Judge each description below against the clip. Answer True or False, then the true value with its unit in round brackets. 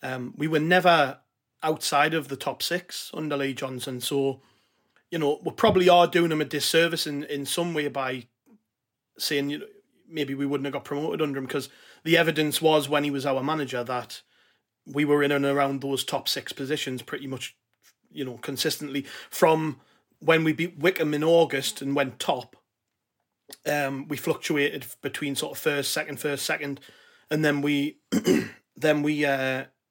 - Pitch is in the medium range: True (145 Hz)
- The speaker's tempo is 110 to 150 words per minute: False (175 wpm)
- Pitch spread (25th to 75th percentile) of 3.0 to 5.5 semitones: False (2.4 semitones)